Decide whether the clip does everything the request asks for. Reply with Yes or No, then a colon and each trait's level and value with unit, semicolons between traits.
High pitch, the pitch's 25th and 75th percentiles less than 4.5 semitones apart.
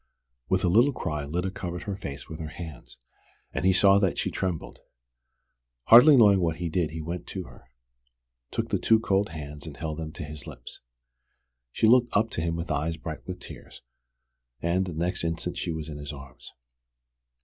No: very low, 85 Hz; average, 3.4 semitones